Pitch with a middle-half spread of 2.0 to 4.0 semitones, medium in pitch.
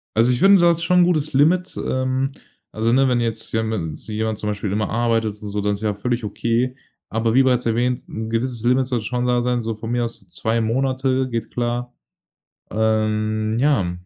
No: average, 2.8 semitones; low, 115 Hz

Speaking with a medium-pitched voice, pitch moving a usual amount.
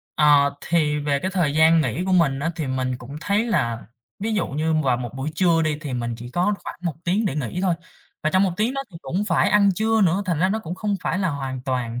No: medium, 160 Hz; wide, 5.7 semitones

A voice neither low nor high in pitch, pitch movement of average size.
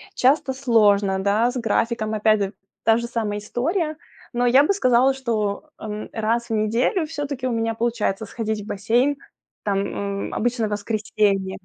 No: high, 225 Hz; average, 3.1 semitones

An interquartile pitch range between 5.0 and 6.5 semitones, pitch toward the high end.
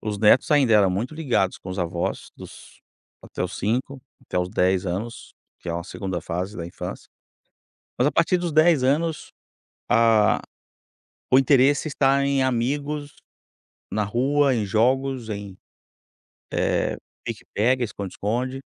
No: wide, 5.6 semitones; low, 120 Hz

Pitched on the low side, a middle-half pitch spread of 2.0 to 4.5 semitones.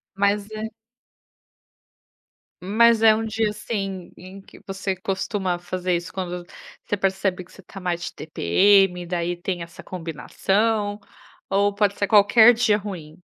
No: high, 195 Hz; narrow, 2.6 semitones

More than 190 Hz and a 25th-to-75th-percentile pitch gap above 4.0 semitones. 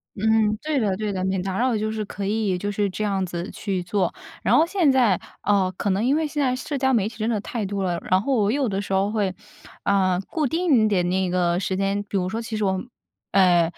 No: high, 205 Hz; average, 3.2 semitones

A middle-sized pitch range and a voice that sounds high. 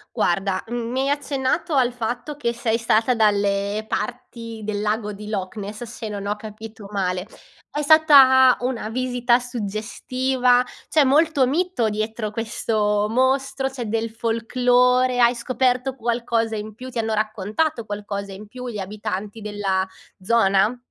Yes: average, 3.2 semitones; high, 230 Hz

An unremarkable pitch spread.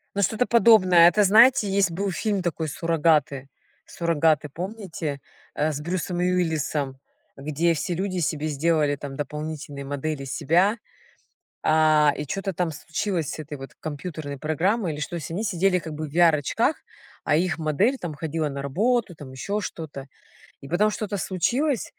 Yes: average, 4.2 semitones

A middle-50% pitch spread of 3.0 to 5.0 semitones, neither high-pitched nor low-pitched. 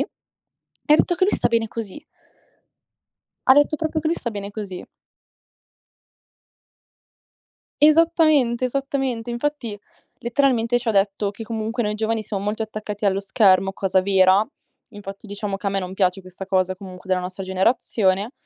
No: average, 3.8 semitones; high, 210 Hz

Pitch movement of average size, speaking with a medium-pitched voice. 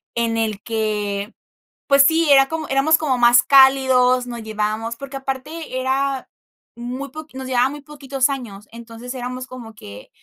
No: average, 3.0 semitones; very high, 255 Hz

